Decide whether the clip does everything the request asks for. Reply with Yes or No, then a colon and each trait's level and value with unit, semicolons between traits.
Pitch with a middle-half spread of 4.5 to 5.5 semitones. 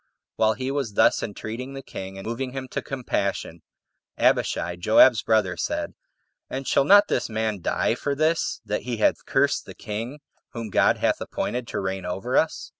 Yes: average, 5.0 semitones